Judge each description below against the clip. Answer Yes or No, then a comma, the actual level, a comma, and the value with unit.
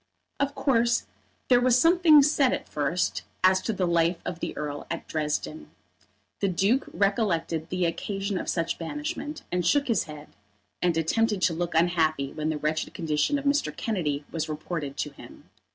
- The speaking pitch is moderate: Yes, medium, 180 Hz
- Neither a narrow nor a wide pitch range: No, wide, 6.8 semitones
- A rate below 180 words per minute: Yes, average, 170 wpm